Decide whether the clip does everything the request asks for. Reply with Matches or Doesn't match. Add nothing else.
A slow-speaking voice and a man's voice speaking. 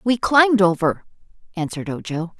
Doesn't match